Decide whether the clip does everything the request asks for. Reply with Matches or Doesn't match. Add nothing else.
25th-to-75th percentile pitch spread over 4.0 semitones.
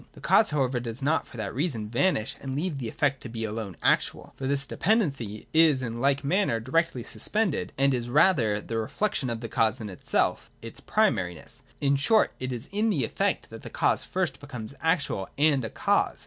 Matches